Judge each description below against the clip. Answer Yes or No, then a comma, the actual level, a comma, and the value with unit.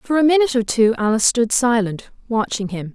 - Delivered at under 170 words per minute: No, fast, 205 wpm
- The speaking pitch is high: Yes, high, 235 Hz